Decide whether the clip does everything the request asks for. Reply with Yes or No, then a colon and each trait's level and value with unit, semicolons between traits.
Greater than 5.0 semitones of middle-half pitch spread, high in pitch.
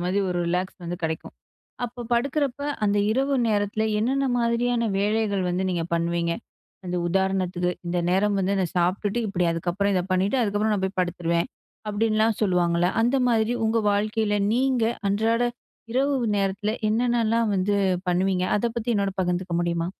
No: average, 4.0 semitones; high, 200 Hz